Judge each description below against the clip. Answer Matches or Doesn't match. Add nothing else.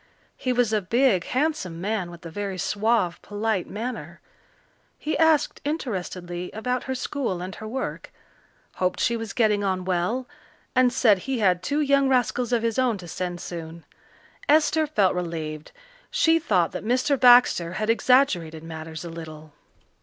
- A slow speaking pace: Doesn't match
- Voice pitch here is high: Matches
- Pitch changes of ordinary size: Doesn't match